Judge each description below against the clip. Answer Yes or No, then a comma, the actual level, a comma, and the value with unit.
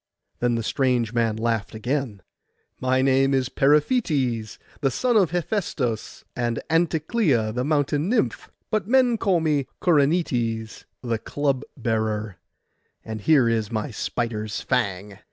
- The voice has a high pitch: No, low, 130 Hz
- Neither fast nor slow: No, slow, 130 wpm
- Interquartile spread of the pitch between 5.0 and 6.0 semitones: Yes, average, 5.3 semitones